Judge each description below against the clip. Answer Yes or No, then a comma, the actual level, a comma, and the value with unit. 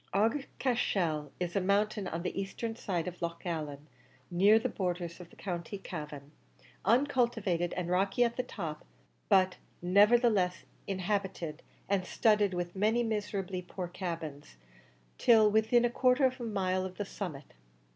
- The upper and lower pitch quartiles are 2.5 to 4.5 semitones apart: Yes, average, 3.8 semitones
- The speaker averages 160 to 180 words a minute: No, average, 150 wpm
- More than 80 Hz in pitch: Yes, high, 190 Hz